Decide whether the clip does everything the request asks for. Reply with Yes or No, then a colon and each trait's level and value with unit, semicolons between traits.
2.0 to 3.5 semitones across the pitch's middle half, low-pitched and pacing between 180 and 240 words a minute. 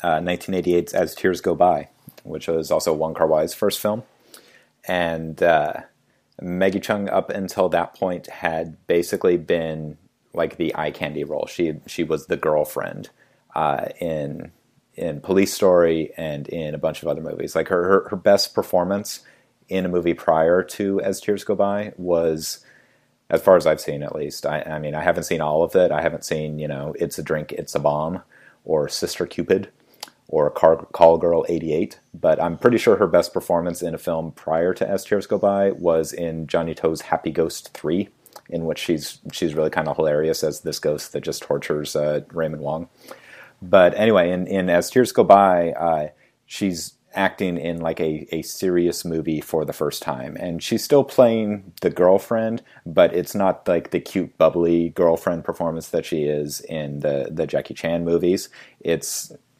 Yes: average, 3.1 semitones; very low, 85 Hz; average, 185 wpm